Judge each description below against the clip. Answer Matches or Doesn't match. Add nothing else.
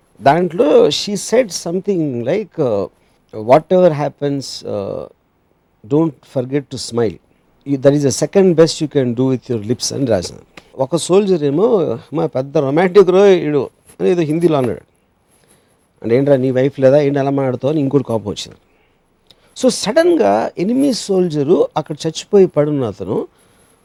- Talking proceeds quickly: Matches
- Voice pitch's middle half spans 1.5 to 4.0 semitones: Doesn't match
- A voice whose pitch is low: Doesn't match